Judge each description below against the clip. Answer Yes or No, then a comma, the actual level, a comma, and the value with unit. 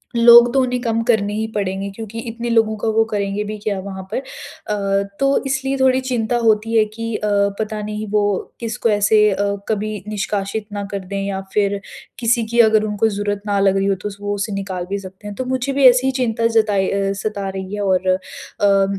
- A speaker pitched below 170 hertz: No, high, 210 Hz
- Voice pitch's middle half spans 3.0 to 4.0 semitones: No, narrow, 2.4 semitones